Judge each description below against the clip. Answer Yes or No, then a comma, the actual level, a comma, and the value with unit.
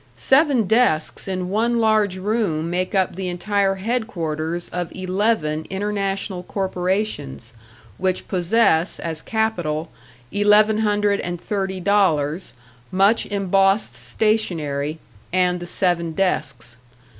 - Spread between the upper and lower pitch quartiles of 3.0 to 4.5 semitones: Yes, average, 3.5 semitones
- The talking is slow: Yes, slow, 110 wpm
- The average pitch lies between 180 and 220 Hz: Yes, high, 190 Hz